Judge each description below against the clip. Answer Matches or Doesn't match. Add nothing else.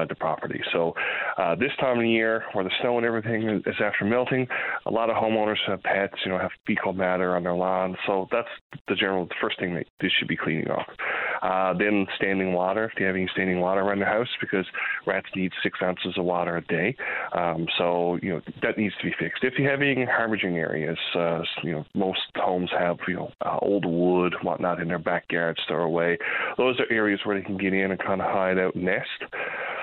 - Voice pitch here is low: Matches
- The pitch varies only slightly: Doesn't match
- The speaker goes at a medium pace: Doesn't match